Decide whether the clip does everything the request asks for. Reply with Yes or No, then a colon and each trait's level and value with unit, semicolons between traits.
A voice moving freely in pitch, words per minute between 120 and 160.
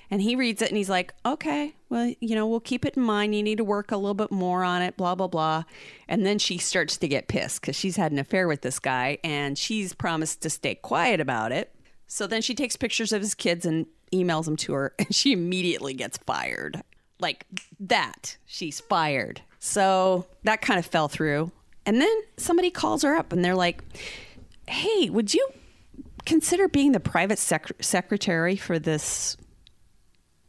No: wide, 5.8 semitones; average, 195 wpm